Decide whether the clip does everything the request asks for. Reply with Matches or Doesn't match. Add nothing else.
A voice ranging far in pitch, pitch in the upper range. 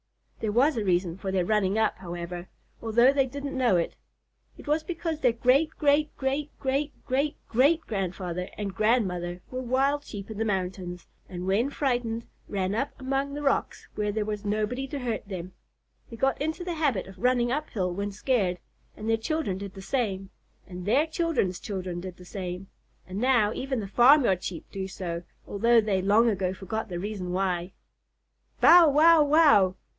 Matches